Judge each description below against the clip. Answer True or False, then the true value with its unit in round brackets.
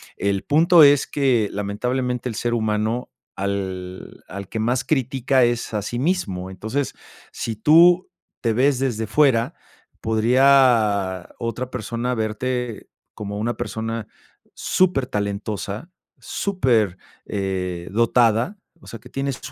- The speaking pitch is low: True (115 Hz)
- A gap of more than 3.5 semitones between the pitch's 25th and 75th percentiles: True (4.0 semitones)